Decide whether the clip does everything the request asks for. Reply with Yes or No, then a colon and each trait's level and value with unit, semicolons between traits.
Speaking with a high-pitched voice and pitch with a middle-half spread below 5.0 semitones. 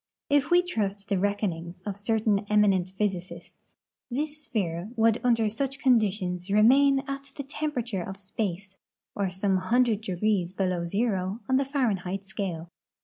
Yes: high, 205 Hz; average, 4.6 semitones